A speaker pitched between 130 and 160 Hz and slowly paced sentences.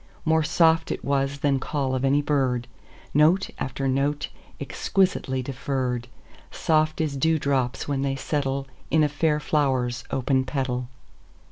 Yes: medium, 140 Hz; slow, 125 wpm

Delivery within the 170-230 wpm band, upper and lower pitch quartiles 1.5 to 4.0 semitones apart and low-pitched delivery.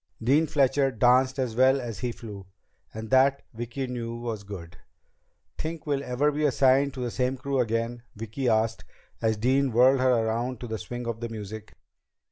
Yes: average, 180 wpm; average, 2.9 semitones; low, 125 Hz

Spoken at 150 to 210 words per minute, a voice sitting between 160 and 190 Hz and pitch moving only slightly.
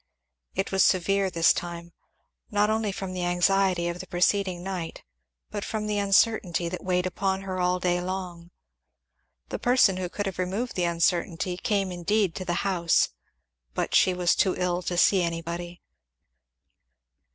Yes: average, 160 wpm; medium, 185 Hz; narrow, 1.9 semitones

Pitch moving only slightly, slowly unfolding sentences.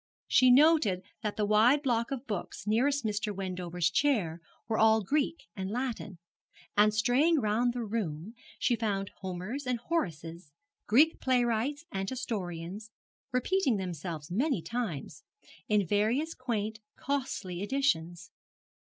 No: wide, 5.4 semitones; slow, 125 wpm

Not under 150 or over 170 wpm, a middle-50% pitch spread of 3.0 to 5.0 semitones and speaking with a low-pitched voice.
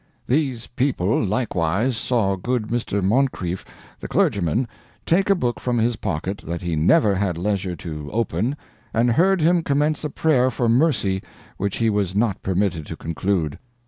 No: average, 160 wpm; wide, 5.6 semitones; low, 110 Hz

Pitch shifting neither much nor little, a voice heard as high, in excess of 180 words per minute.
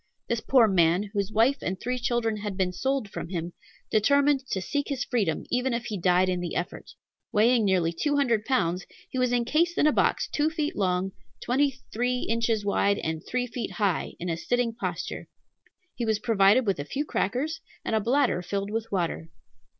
Yes: average, 4.9 semitones; high, 220 Hz; average, 195 wpm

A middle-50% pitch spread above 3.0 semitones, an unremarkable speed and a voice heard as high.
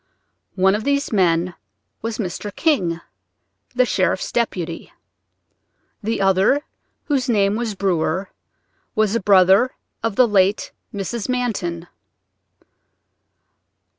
No: average, 4.1 semitones; slow, 105 wpm; high, 200 Hz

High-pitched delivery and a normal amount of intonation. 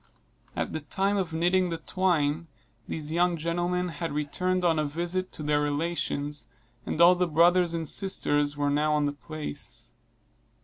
No: medium, 165 Hz; average, 3.1 semitones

